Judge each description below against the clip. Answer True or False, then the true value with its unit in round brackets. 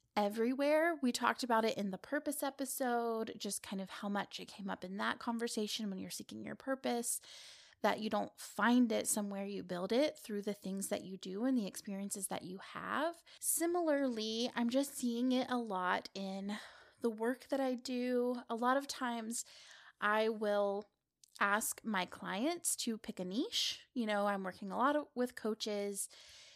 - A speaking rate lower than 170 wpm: False (180 wpm)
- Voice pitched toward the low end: False (230 Hz)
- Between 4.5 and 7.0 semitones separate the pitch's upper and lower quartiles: False (3.9 semitones)